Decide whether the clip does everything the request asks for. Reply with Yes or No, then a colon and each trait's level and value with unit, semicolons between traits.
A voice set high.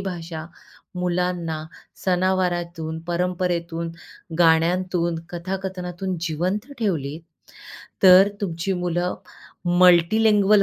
No: medium, 180 Hz